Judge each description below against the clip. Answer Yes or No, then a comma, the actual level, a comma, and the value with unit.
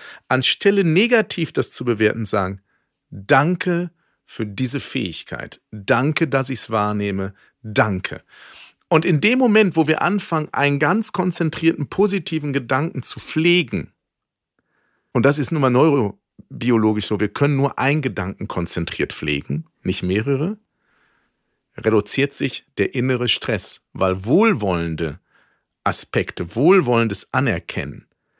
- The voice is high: No, low, 135 Hz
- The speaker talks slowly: Yes, slow, 120 wpm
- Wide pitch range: Yes, wide, 7.3 semitones